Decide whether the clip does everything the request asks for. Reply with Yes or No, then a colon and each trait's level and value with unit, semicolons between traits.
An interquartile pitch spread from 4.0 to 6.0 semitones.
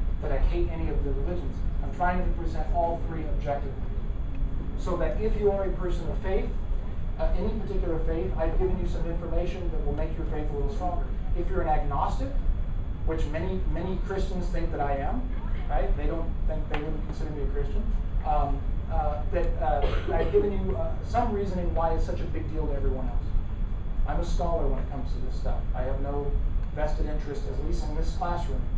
No: average, 3.1 semitones